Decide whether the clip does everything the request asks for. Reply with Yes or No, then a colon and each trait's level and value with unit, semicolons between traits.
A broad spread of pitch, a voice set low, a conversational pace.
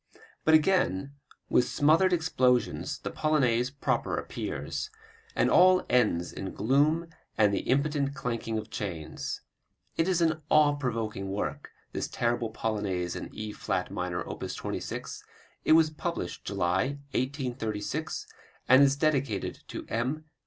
No: wide, 6.2 semitones; low, 130 Hz; slow, 130 wpm